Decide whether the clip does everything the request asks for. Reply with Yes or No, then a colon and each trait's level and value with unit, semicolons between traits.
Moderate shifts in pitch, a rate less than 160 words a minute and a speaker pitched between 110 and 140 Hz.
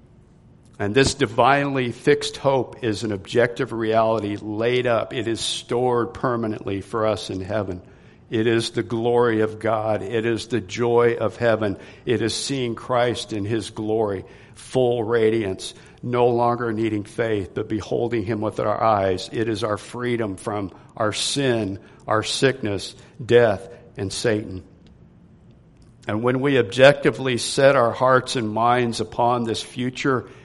No: narrow, 2.2 semitones; average, 145 wpm; low, 115 Hz